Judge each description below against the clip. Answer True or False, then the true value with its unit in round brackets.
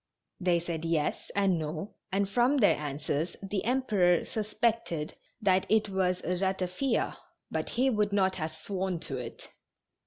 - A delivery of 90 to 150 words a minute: True (145 wpm)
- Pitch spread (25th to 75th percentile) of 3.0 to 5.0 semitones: True (3.8 semitones)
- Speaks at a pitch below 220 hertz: True (190 Hz)